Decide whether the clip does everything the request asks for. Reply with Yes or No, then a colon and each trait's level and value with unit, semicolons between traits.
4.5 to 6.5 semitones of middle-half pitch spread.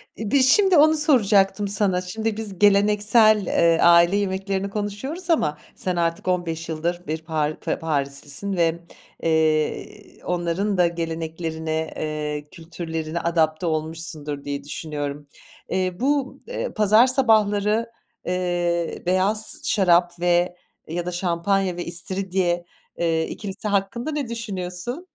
No: average, 4.1 semitones